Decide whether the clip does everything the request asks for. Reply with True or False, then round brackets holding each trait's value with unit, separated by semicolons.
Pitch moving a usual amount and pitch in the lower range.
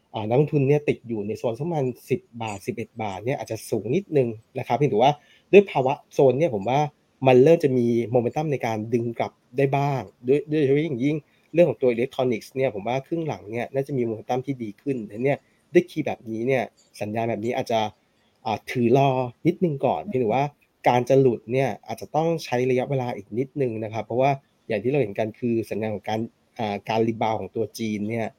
True (3.9 semitones; 125 Hz)